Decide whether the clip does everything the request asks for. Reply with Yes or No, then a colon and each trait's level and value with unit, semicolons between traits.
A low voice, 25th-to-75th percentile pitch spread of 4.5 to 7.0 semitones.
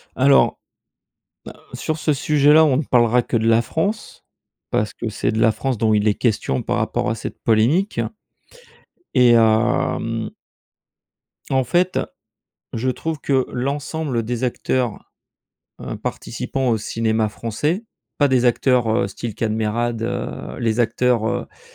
No: low, 120 Hz; average, 3.7 semitones